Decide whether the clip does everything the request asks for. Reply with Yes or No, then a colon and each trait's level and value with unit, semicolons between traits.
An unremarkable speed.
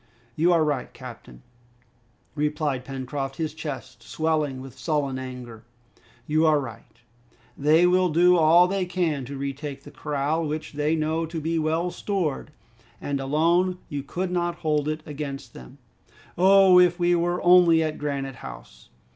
Yes: average, 155 wpm